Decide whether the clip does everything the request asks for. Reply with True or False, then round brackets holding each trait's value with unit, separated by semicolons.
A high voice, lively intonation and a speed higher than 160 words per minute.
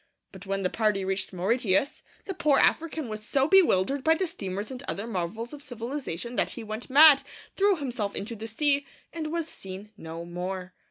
True (230 Hz; 6.8 semitones; 185 wpm)